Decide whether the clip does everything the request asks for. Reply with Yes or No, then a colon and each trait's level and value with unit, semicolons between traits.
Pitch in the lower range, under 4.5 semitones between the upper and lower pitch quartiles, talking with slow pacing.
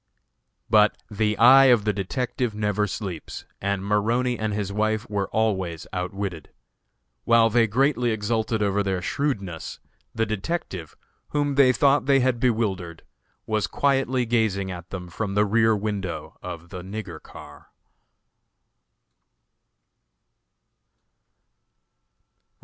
Yes: low, 105 Hz; average, 3.5 semitones; slow, 115 wpm